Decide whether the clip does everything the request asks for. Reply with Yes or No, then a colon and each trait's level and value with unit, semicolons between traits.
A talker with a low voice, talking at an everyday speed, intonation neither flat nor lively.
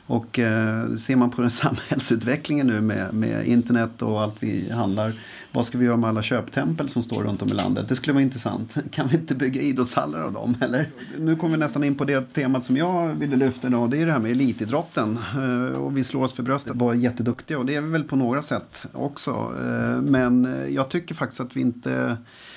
No: low, 125 Hz; fast, 220 wpm; average, 3.0 semitones